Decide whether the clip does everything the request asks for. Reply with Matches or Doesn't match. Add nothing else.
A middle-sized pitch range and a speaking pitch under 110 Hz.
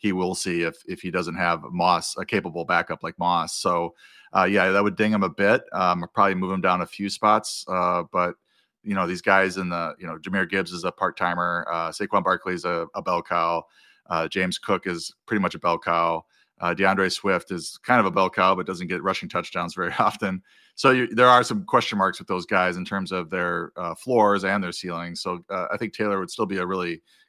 Doesn't match